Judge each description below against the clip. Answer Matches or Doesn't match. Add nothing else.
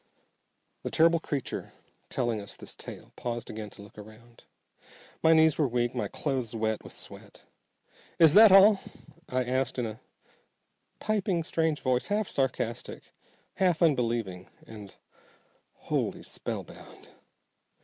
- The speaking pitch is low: Matches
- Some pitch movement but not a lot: Doesn't match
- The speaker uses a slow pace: Matches